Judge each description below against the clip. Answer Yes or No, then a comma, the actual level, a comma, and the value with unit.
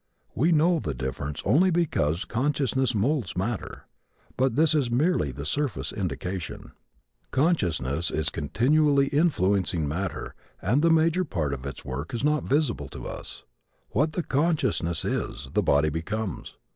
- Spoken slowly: No, average, 145 wpm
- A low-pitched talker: Yes, low, 115 Hz